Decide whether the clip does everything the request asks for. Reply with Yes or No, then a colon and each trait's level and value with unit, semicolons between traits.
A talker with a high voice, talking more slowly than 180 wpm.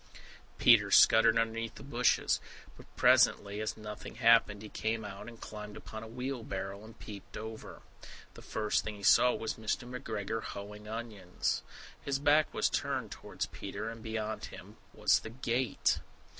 No: low, 110 Hz; average, 155 wpm